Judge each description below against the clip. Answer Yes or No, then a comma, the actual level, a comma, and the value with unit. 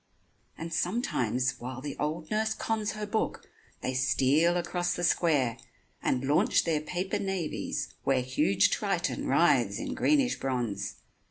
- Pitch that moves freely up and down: Yes, wide, 6.7 semitones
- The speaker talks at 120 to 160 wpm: Yes, average, 140 wpm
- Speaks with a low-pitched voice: No, medium, 155 Hz